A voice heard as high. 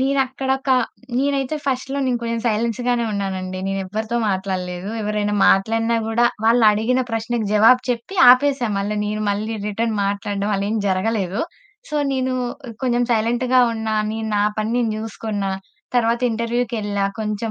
Yes: high, 225 Hz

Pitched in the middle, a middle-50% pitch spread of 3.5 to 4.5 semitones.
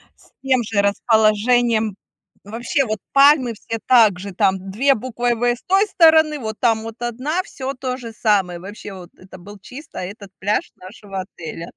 No: high, 225 Hz; average, 4.1 semitones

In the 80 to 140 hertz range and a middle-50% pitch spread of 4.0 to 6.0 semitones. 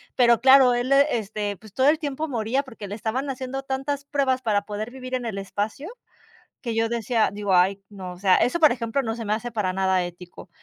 No: high, 230 Hz; average, 4.5 semitones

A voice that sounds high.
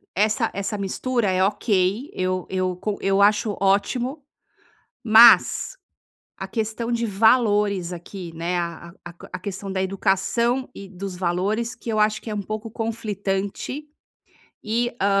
Yes: high, 200 Hz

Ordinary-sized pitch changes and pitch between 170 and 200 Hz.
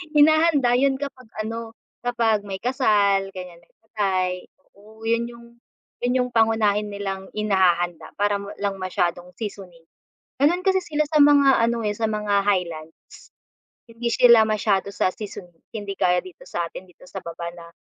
No: average, 4.1 semitones; high, 210 Hz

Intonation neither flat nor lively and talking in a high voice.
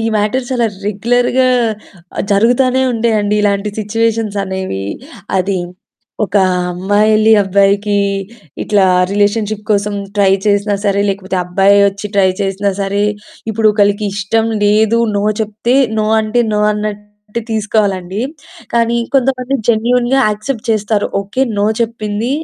No: narrow, 2.1 semitones; high, 210 Hz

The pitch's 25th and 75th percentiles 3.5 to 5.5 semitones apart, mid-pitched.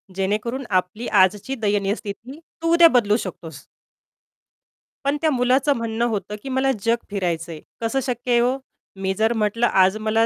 No: average, 4.2 semitones; high, 225 Hz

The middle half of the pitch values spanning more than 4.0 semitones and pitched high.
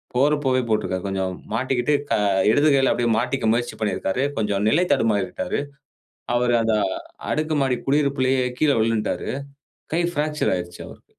No: average, 4.5 semitones; low, 125 Hz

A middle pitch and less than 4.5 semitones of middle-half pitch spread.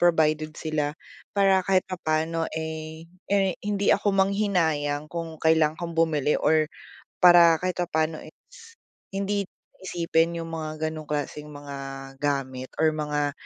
Yes: medium, 160 Hz; average, 3.0 semitones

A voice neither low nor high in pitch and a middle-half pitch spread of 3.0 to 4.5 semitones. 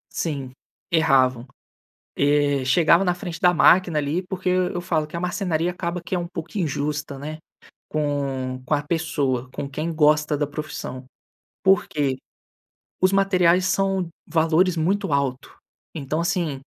Yes: medium, 155 Hz; average, 3.8 semitones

